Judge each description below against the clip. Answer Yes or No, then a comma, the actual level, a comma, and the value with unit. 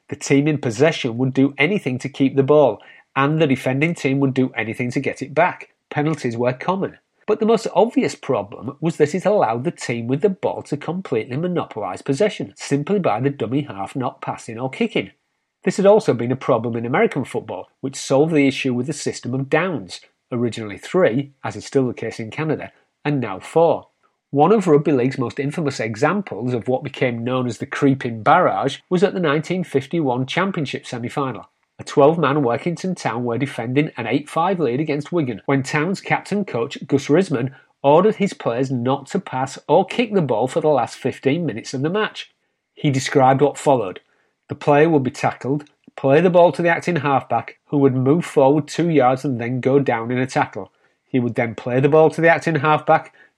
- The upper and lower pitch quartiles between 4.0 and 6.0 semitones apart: No, average, 3.6 semitones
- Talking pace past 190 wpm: Yes, average, 200 wpm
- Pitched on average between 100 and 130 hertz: No, medium, 140 Hz